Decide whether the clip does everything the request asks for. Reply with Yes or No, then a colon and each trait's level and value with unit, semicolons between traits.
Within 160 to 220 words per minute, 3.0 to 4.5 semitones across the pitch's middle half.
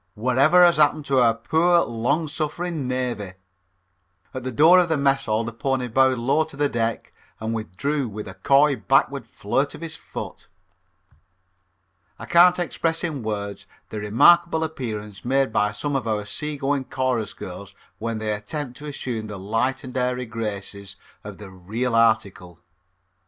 No: average, 165 wpm; average, 5.1 semitones